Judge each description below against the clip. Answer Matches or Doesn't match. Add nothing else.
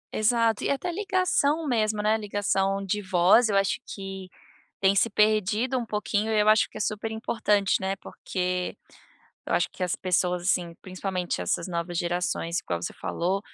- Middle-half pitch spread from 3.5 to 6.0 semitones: Doesn't match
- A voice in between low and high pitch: Doesn't match